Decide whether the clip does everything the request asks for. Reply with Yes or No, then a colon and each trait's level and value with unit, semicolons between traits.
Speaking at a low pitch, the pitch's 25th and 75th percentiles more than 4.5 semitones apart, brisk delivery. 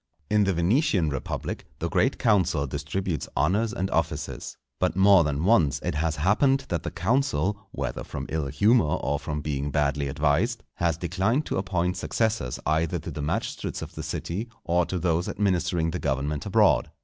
No: very low, 85 Hz; average, 5.0 semitones; average, 175 wpm